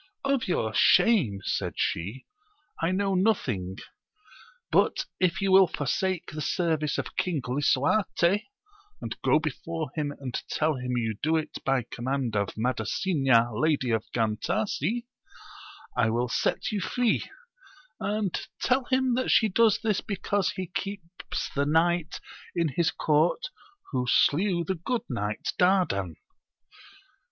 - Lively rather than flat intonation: Yes, wide, 7.4 semitones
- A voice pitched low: No, medium, 160 Hz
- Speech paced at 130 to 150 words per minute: Yes, slow, 135 wpm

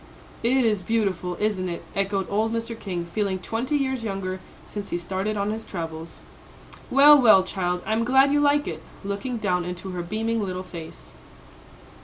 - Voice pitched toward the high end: Yes, high, 200 Hz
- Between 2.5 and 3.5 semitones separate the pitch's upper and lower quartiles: No, average, 3.9 semitones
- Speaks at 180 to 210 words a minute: No, average, 170 wpm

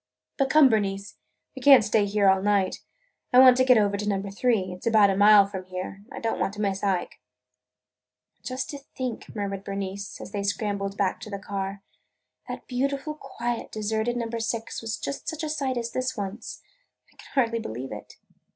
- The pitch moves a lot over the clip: No, average, 3.9 semitones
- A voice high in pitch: Yes, high, 210 Hz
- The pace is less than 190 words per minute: No, average, 200 wpm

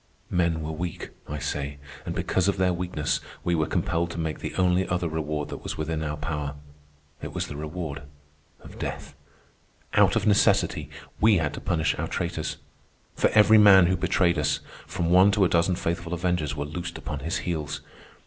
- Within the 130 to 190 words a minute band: Yes, average, 185 wpm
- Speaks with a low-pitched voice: Yes, very low, 85 Hz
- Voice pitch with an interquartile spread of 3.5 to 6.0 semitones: No, average, 2.9 semitones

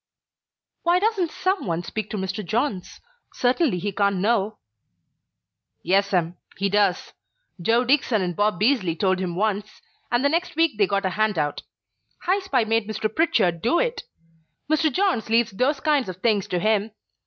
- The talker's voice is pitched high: Yes, high, 215 Hz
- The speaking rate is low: No, average, 175 wpm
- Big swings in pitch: Yes, wide, 6.7 semitones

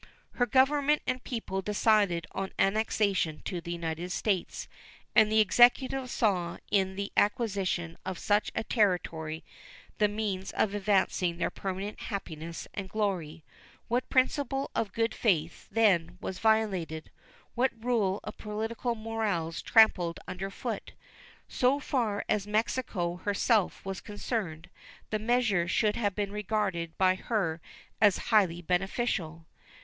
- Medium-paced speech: No, slow, 130 wpm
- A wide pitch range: No, average, 3.8 semitones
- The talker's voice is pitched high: Yes, high, 205 Hz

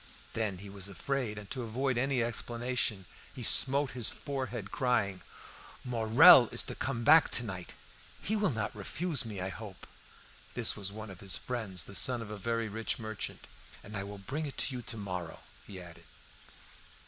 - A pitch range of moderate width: Yes, average, 4.1 semitones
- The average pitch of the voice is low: Yes, low, 110 Hz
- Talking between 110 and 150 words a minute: No, average, 180 wpm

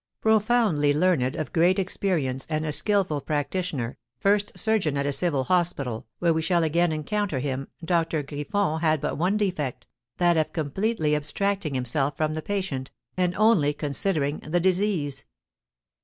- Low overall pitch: No, medium, 160 Hz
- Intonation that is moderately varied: Yes, average, 4.5 semitones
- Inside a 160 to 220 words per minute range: No, average, 150 wpm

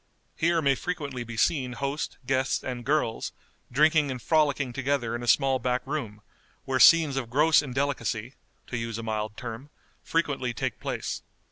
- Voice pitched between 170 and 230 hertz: No, low, 130 Hz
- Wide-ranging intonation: No, average, 3.5 semitones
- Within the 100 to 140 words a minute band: No, average, 160 wpm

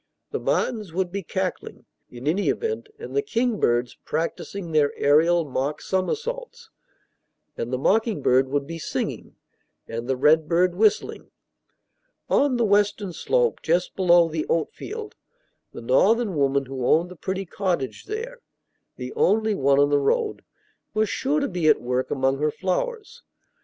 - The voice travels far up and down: Yes, wide, 8.2 semitones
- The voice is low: No, medium, 180 Hz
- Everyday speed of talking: Yes, average, 150 wpm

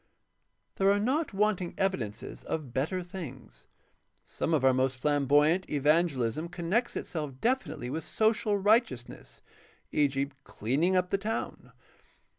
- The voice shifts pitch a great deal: Yes, wide, 6.3 semitones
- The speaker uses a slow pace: Yes, slow, 130 wpm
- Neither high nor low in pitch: Yes, medium, 165 Hz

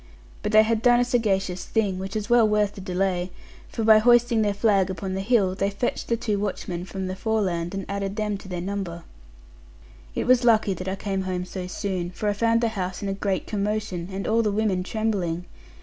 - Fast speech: Yes, fast, 220 wpm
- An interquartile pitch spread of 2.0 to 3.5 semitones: Yes, narrow, 2.6 semitones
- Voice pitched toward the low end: No, high, 200 Hz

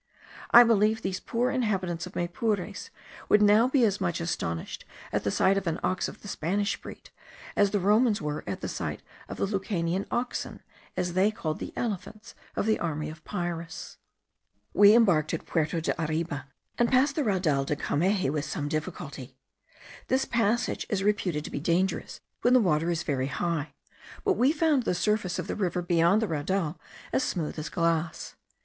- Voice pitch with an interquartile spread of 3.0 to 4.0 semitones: No, average, 4.7 semitones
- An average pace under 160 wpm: No, average, 180 wpm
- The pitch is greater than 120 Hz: Yes, medium, 185 Hz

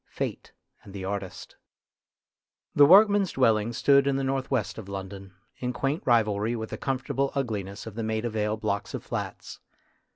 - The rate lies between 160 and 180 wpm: Yes, average, 165 wpm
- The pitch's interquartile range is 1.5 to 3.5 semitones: No, average, 4.9 semitones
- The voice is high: No, low, 115 Hz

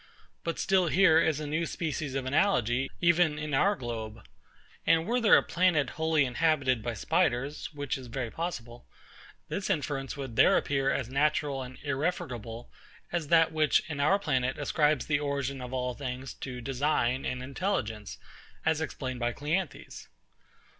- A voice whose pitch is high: No, medium, 140 Hz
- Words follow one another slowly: No, average, 160 wpm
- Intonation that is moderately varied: Yes, average, 4.0 semitones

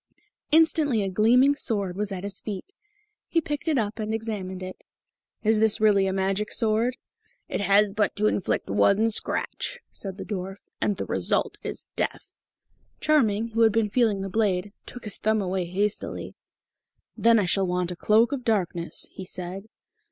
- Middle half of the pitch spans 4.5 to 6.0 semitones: No, average, 2.8 semitones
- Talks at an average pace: Yes, average, 175 wpm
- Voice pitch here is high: Yes, high, 210 Hz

